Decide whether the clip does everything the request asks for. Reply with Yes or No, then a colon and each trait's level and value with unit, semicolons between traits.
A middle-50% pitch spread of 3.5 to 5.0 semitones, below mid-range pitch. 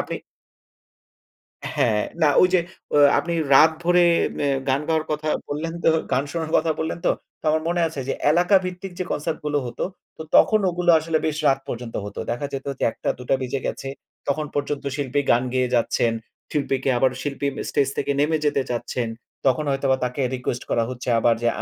No: average, 3.8 semitones; medium, 145 Hz